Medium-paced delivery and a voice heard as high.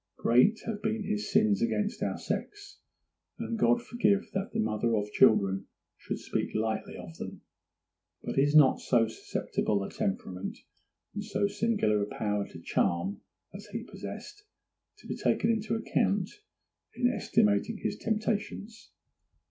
Yes: average, 145 wpm; high, 200 Hz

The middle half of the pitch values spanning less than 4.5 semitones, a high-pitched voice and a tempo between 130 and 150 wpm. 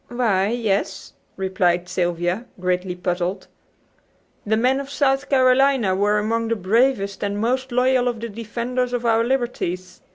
No: average, 4.9 semitones; high, 225 Hz; average, 140 wpm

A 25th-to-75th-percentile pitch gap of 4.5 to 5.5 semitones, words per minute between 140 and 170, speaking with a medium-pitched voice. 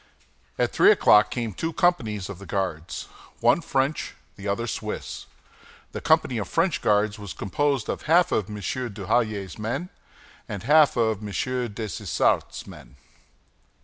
No: average, 5.1 semitones; average, 145 wpm; low, 110 Hz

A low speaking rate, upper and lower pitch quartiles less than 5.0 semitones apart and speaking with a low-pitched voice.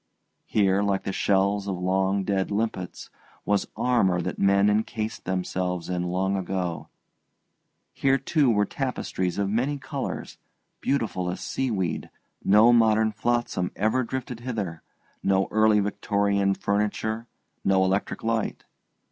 Yes: slow, 125 wpm; average, 2.9 semitones; low, 100 Hz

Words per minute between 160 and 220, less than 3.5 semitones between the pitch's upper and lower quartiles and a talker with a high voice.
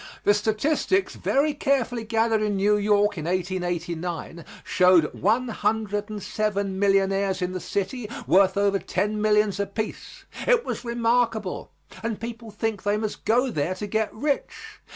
No: average, 150 wpm; average, 2.8 semitones; high, 210 Hz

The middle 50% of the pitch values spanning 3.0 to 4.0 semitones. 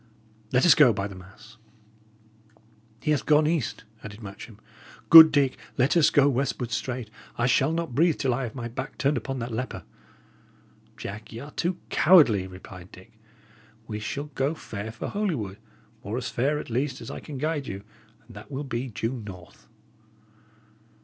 No: average, 5.3 semitones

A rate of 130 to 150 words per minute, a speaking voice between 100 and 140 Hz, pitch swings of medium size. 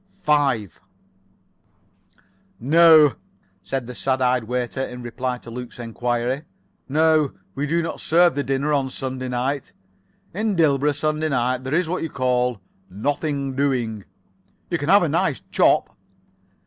Yes: average, 140 wpm; low, 135 Hz; average, 3.3 semitones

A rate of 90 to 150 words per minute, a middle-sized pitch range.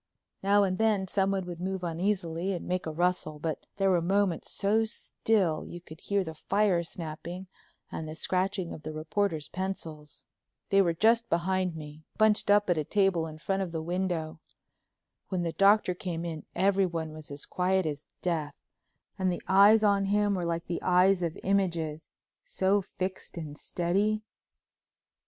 No: average, 170 wpm; average, 3.2 semitones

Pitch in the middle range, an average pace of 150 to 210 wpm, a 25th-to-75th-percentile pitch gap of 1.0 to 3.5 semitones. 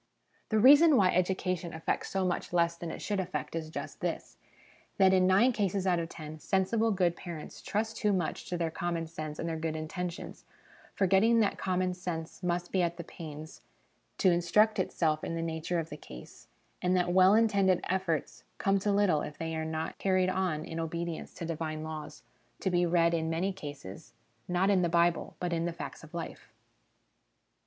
Yes: medium, 175 Hz; average, 190 wpm; average, 2.7 semitones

